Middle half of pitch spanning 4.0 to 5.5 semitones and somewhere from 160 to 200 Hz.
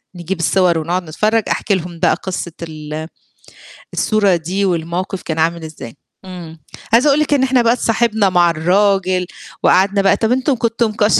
Yes: average, 4.4 semitones; medium, 185 Hz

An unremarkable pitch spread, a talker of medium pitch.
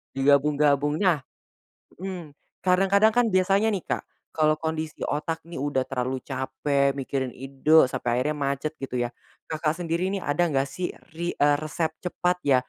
Yes: average, 4.0 semitones; medium, 150 Hz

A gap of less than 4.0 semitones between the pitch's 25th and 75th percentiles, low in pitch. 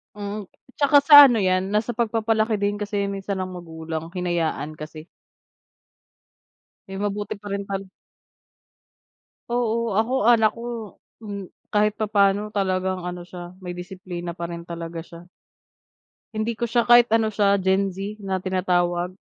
No: average, 3.3 semitones; high, 200 Hz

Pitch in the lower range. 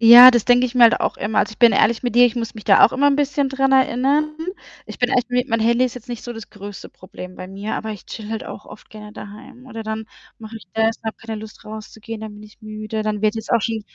No: high, 225 Hz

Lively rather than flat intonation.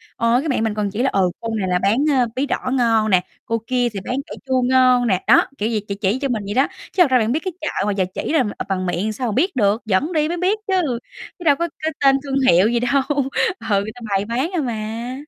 No: average, 4.6 semitones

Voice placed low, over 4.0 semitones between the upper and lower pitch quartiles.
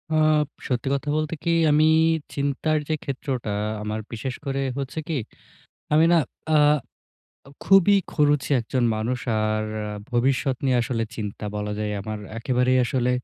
Yes: low, 130 Hz; average, 4.4 semitones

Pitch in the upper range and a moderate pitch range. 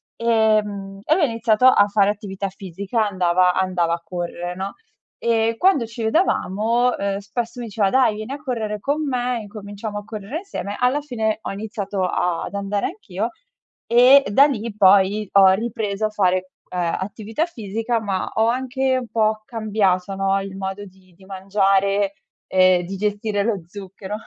Yes: high, 205 Hz; average, 3.0 semitones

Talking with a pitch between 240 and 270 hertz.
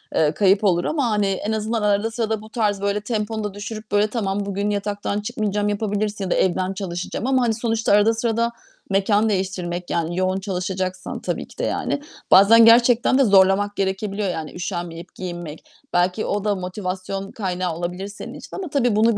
No: high, 205 Hz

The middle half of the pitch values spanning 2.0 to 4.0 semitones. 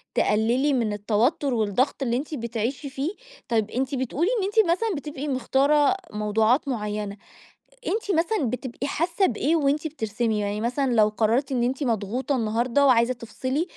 No: average, 4.6 semitones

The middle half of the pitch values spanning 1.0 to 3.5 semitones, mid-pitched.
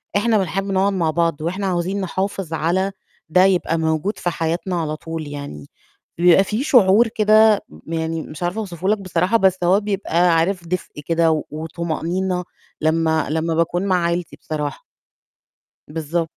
Yes: average, 3.0 semitones; medium, 175 Hz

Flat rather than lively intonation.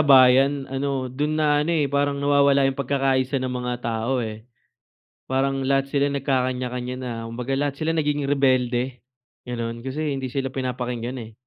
Yes: narrow, 2.0 semitones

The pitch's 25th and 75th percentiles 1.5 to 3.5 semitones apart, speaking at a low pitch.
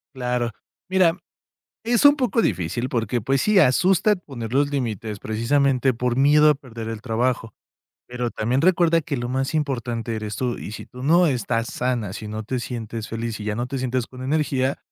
No: average, 4.0 semitones; low, 125 Hz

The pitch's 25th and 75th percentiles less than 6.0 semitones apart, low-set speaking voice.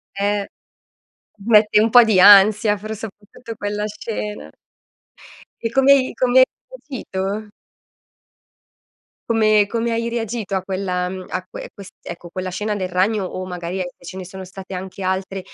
No: average, 2.7 semitones; high, 205 Hz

